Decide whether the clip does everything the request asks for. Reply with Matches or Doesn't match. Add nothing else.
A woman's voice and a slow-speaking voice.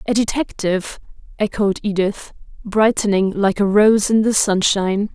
Matches